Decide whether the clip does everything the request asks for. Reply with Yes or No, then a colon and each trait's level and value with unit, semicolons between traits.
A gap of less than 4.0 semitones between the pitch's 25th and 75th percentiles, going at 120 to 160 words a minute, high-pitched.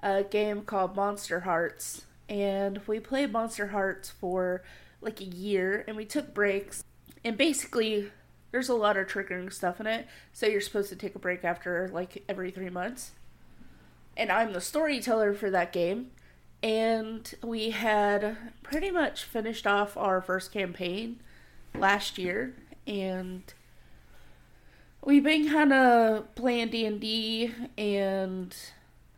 Yes: average, 3.5 semitones; average, 140 wpm; high, 205 Hz